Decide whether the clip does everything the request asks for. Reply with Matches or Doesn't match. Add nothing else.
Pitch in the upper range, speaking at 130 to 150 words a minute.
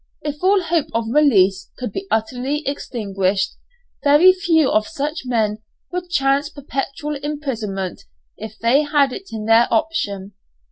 Matches